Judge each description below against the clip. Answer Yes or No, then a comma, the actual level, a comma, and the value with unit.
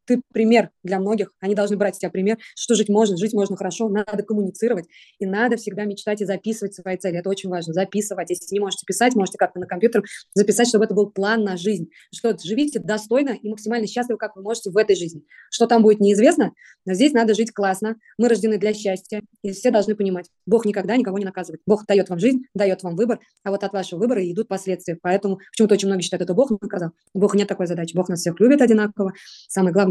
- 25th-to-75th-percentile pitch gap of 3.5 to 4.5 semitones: No, narrow, 2.6 semitones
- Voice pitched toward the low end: No, high, 205 Hz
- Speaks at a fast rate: Yes, fast, 225 wpm